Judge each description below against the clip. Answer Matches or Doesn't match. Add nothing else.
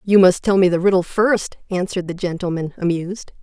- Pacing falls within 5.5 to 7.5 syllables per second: Matches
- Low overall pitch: Doesn't match